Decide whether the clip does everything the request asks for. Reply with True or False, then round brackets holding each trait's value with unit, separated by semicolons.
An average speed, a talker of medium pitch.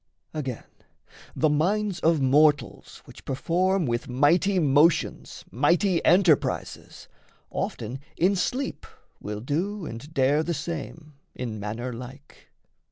False (110 wpm; 150 Hz)